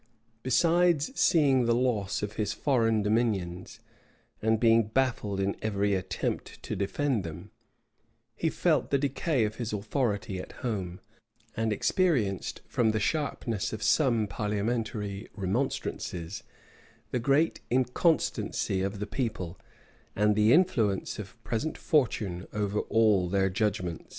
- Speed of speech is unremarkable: No, slow, 125 wpm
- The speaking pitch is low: Yes, low, 110 Hz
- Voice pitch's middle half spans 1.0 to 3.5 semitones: No, average, 4.0 semitones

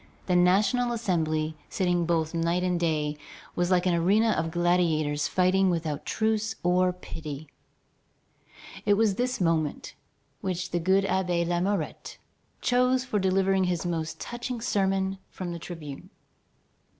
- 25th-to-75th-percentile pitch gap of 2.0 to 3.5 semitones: Yes, average, 2.7 semitones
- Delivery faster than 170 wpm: No, slow, 135 wpm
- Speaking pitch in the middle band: Yes, medium, 180 Hz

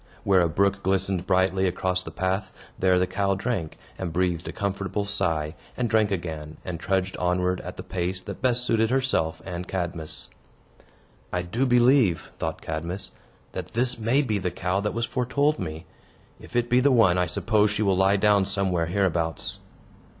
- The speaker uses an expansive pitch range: No, average, 3.3 semitones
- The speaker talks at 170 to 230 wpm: Yes, average, 180 wpm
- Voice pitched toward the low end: Yes, very low, 95 Hz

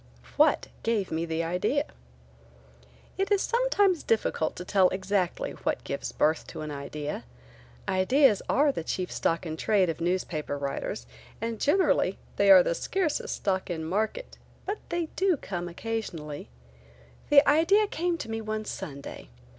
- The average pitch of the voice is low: No, high, 195 Hz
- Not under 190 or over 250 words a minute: No, average, 150 wpm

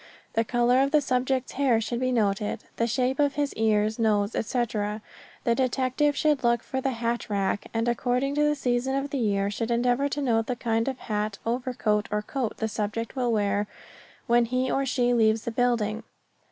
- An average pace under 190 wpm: No, average, 195 wpm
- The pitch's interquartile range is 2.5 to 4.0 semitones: Yes, average, 3.1 semitones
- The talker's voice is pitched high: Yes, high, 240 Hz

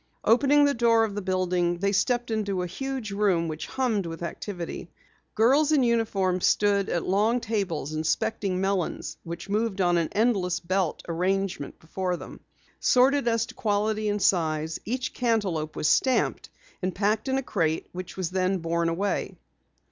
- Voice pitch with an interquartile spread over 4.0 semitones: Yes, average, 4.4 semitones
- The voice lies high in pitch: Yes, high, 195 Hz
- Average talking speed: Yes, average, 165 wpm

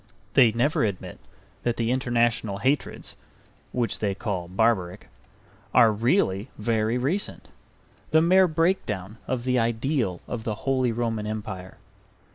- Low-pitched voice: Yes, low, 115 Hz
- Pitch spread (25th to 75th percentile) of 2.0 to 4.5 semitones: Yes, average, 3.4 semitones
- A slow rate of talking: Yes, slow, 125 wpm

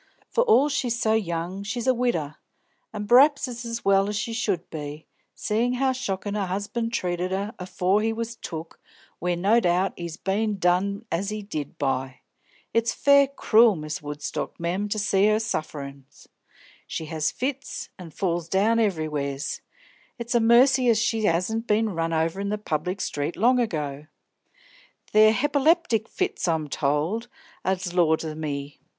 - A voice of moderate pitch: No, high, 200 Hz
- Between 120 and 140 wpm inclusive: No, average, 160 wpm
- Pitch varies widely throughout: Yes, wide, 5.9 semitones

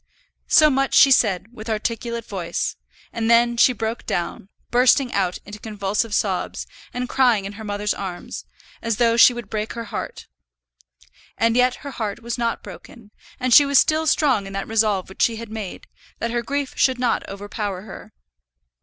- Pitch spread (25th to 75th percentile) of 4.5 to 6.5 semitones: No, average, 3.2 semitones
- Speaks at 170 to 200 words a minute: Yes, average, 180 wpm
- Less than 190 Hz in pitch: No, high, 230 Hz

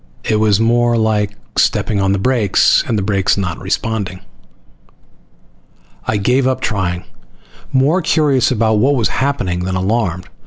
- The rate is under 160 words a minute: Yes, average, 145 wpm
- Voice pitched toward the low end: Yes, low, 110 Hz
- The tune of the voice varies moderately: Yes, average, 4.3 semitones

